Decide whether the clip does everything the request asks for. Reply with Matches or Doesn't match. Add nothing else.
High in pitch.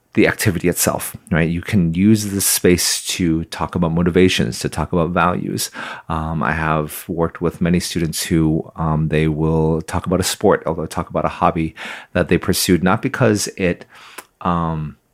Doesn't match